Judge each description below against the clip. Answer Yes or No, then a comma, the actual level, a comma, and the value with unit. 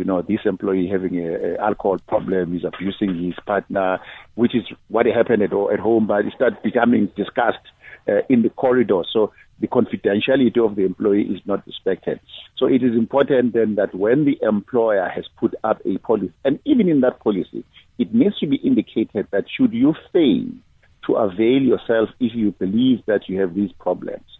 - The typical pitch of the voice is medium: No, low, 110 Hz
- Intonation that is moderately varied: No, wide, 6.1 semitones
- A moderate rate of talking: Yes, average, 190 wpm